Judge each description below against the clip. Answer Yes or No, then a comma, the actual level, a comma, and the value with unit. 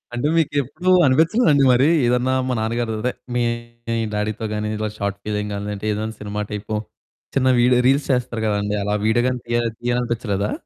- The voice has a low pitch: Yes, low, 115 Hz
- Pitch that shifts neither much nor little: Yes, average, 3.2 semitones